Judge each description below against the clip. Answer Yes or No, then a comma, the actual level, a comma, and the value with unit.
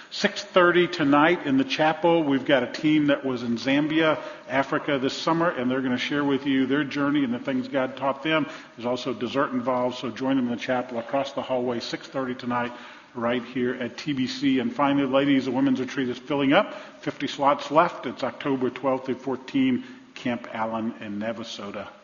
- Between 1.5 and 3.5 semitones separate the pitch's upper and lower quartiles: Yes, average, 3.1 semitones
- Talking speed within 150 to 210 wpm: Yes, average, 200 wpm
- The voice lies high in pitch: No, low, 135 Hz